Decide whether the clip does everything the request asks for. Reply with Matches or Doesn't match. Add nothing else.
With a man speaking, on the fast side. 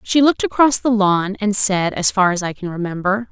Doesn't match